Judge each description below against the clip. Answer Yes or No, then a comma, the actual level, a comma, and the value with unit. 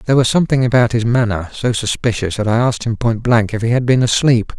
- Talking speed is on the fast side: Yes, fast, 250 wpm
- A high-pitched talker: No, low, 115 Hz